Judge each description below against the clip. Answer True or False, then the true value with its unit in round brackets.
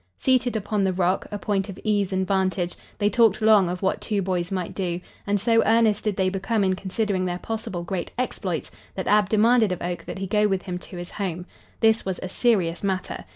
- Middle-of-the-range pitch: False (195 Hz)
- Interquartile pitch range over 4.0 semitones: False (2.6 semitones)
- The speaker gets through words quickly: True (220 wpm)